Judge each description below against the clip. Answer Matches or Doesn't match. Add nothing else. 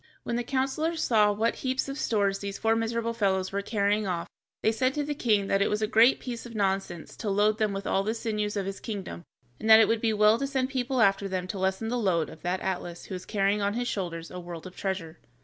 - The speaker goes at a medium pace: Doesn't match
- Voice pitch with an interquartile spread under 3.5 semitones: Matches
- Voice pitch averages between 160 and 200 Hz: Doesn't match